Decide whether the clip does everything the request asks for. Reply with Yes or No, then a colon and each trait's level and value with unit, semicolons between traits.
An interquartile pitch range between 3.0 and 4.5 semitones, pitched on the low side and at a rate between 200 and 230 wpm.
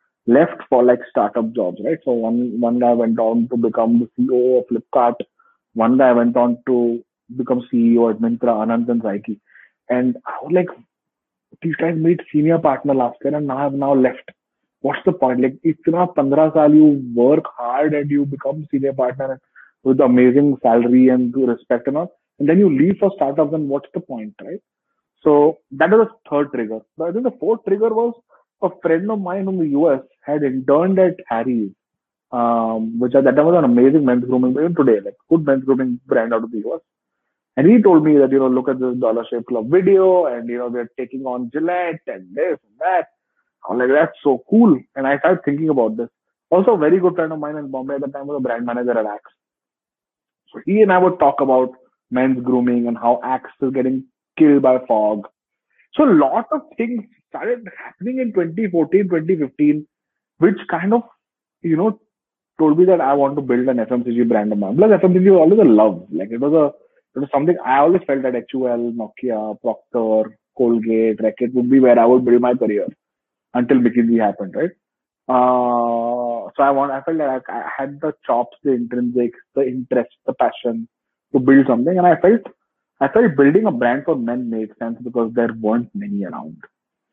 No: average, 5.3 semitones; low, 130 Hz; fast, 205 wpm